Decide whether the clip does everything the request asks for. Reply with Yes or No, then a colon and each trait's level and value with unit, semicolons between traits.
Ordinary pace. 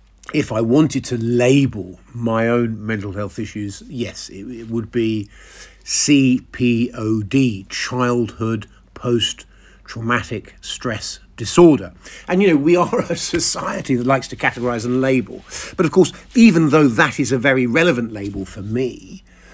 Yes: average, 155 wpm